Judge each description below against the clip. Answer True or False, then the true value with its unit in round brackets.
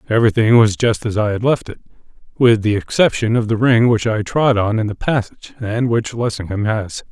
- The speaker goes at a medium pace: False (210 wpm)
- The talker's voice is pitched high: False (110 Hz)